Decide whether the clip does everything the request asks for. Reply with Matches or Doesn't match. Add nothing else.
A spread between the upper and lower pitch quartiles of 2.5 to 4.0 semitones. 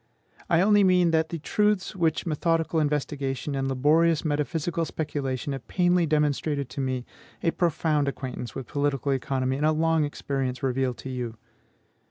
Matches